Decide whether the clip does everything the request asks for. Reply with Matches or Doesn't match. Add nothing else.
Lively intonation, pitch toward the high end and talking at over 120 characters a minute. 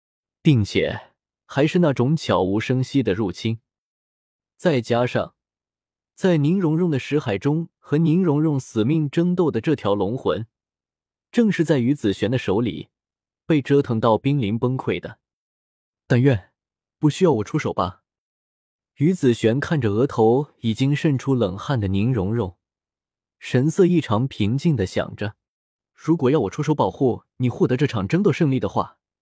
Doesn't match